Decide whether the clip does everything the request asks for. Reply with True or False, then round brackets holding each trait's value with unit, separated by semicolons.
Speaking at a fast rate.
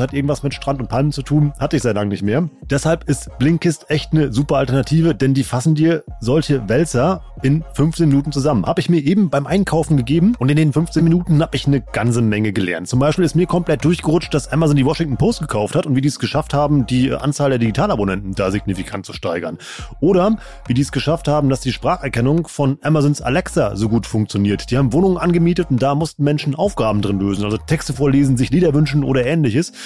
True (220 wpm)